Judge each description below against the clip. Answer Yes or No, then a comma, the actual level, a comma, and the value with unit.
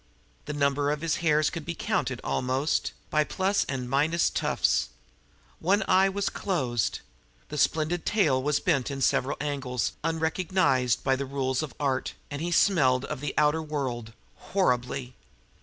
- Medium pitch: Yes, medium, 145 Hz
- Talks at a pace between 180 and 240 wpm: No, average, 155 wpm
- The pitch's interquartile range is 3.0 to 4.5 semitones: Yes, average, 3.9 semitones